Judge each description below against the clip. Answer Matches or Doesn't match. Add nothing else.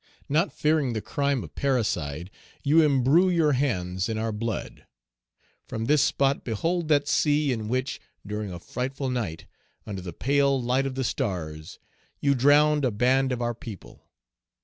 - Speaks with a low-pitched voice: Matches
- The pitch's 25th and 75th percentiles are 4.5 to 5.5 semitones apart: Matches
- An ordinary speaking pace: Matches